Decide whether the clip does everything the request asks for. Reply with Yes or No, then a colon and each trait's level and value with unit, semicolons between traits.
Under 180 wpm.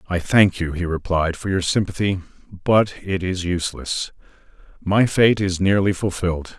Yes: average, 155 wpm